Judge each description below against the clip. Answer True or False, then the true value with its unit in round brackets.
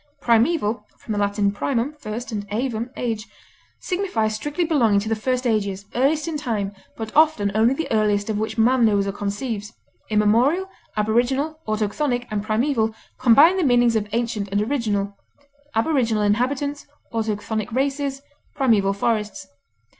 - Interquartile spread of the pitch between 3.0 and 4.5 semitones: True (4.2 semitones)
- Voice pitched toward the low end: False (225 Hz)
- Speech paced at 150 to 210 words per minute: False (140 wpm)